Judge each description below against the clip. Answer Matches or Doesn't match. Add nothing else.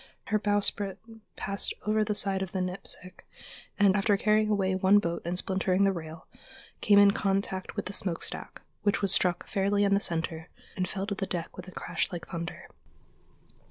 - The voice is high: Matches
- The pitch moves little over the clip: Matches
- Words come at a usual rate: Matches